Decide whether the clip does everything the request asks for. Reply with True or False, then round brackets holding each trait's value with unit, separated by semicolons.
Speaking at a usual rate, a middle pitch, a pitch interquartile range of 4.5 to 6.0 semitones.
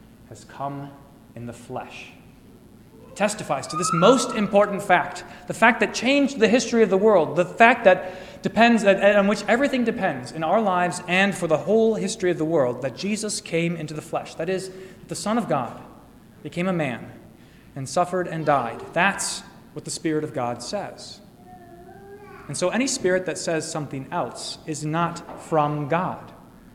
True (175 wpm; 180 Hz; 5.0 semitones)